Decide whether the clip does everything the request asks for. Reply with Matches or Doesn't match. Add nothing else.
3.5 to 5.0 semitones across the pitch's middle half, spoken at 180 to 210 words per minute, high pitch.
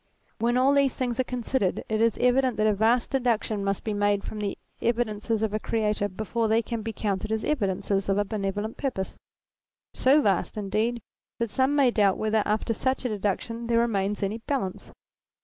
Doesn't match